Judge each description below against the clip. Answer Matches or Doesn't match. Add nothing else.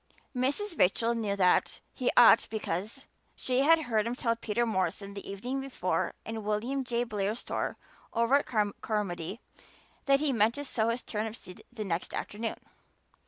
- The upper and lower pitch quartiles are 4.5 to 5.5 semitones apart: Doesn't match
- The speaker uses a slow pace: Doesn't match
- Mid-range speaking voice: Doesn't match